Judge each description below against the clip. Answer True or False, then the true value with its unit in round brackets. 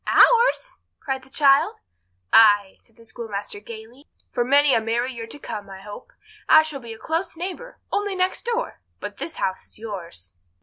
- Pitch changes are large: True (6.6 semitones)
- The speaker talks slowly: False (175 wpm)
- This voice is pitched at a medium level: False (240 Hz)